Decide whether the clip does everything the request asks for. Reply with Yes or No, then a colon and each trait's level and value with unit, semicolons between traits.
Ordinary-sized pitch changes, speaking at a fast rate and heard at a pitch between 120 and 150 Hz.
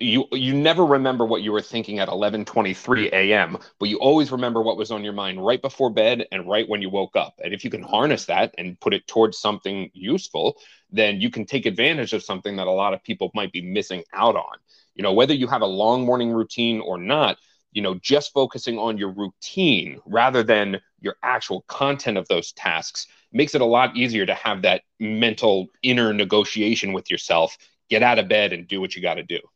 No: average, 3.5 semitones; fast, 220 wpm; low, 110 Hz